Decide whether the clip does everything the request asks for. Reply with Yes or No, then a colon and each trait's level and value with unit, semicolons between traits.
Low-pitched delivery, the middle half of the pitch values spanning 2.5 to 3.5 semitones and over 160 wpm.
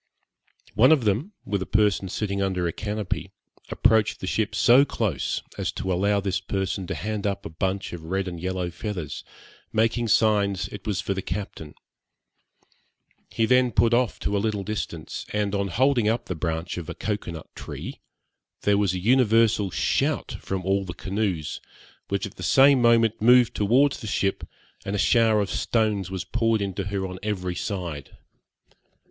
Yes: low, 100 Hz; average, 2.9 semitones; average, 175 wpm